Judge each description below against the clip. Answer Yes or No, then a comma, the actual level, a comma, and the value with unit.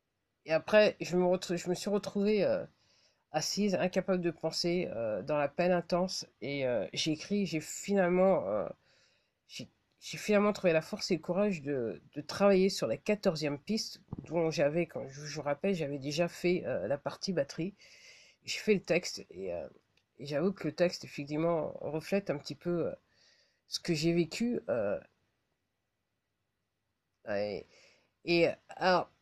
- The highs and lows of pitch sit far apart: No, average, 4.5 semitones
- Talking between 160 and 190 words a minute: Yes, average, 165 wpm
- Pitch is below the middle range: No, medium, 170 Hz